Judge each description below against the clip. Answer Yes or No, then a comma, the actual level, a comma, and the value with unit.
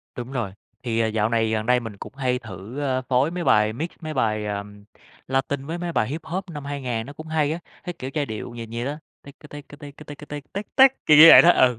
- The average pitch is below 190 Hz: Yes, low, 135 Hz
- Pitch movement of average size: Yes, average, 5.0 semitones